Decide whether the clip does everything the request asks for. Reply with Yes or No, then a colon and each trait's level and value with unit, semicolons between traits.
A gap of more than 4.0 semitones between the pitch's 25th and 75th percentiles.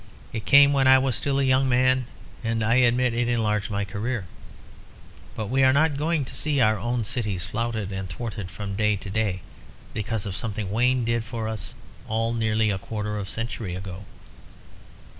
No: average, 3.6 semitones